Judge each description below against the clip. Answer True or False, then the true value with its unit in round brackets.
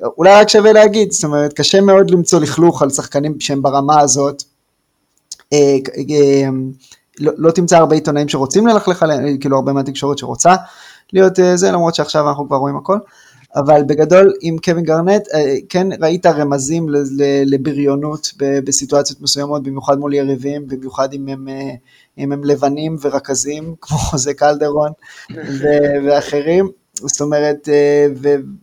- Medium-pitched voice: True (145 Hz)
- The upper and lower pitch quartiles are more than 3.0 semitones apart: False (2.7 semitones)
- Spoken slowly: False (125 wpm)